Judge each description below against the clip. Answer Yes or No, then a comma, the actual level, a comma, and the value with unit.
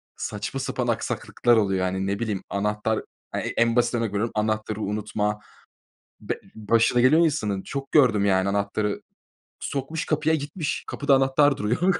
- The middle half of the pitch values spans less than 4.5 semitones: No, average, 4.9 semitones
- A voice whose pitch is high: No, low, 110 Hz